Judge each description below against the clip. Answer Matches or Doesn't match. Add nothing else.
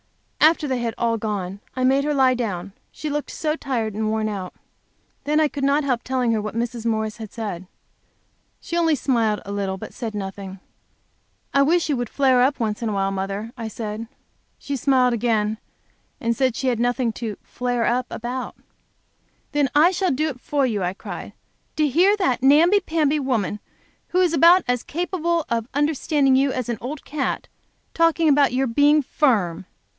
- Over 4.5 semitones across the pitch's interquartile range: Matches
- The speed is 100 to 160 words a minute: Doesn't match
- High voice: Matches